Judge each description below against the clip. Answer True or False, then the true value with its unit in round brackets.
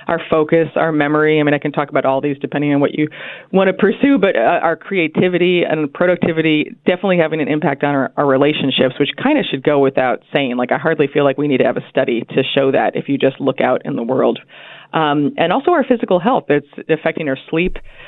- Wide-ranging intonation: False (3.5 semitones)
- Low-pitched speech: False (155 Hz)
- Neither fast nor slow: False (240 wpm)